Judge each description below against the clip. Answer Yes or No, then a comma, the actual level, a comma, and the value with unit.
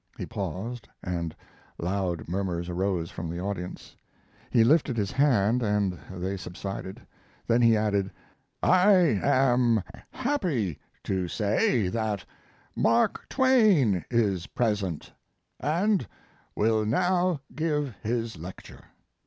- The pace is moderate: No, slow, 110 wpm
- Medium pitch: No, low, 110 Hz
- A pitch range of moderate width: No, wide, 5.8 semitones